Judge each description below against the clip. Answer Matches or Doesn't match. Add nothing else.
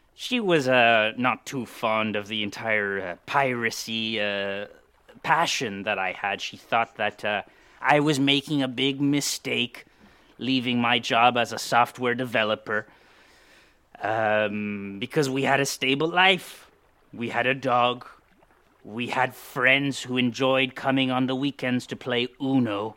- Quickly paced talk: Doesn't match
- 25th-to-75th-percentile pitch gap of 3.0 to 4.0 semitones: Matches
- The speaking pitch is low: Matches